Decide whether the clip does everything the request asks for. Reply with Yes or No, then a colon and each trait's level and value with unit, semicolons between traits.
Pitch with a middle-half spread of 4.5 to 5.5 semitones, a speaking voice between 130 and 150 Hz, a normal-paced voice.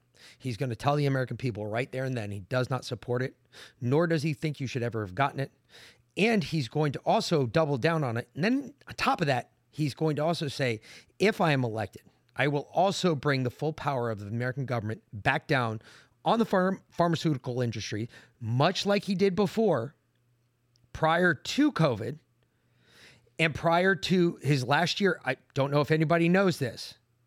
Yes: average, 5.2 semitones; medium, 140 Hz; average, 195 wpm